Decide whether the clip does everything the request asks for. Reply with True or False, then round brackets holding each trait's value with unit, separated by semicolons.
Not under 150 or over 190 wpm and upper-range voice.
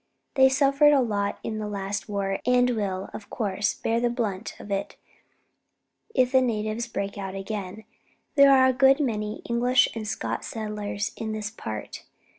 True (170 wpm; 215 Hz)